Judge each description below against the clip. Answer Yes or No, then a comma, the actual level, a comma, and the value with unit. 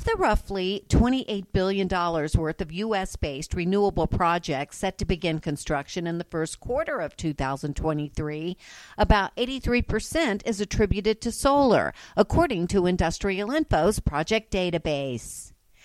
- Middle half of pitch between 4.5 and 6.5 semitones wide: Yes, average, 4.9 semitones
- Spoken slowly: Yes, slow, 125 wpm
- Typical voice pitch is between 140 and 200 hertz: Yes, medium, 185 Hz